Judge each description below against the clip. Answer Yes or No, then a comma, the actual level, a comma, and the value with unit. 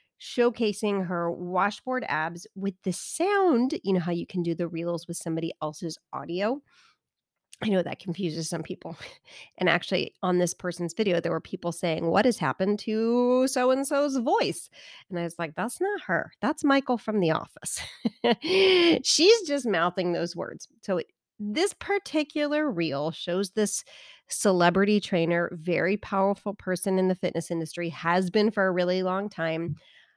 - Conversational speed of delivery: Yes, average, 165 wpm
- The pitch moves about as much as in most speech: No, wide, 6.4 semitones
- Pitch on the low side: No, high, 190 Hz